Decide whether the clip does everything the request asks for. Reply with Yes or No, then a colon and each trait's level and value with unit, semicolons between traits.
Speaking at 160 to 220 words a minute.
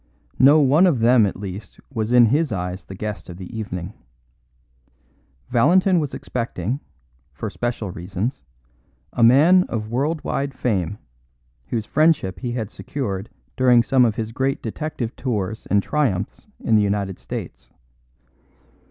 No: average, 145 wpm